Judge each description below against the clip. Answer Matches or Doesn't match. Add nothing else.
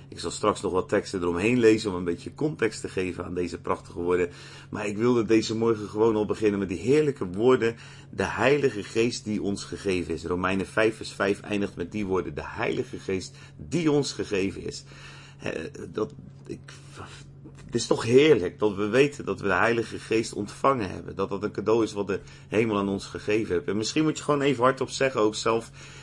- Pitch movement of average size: Matches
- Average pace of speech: Doesn't match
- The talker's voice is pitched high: Doesn't match